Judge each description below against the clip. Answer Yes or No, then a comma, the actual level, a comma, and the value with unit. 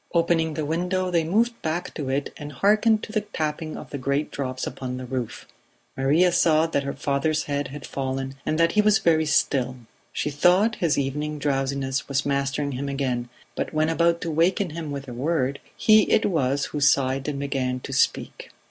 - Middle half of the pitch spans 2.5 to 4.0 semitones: Yes, average, 3.5 semitones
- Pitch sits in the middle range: Yes, medium, 150 Hz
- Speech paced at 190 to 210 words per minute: Yes, average, 195 wpm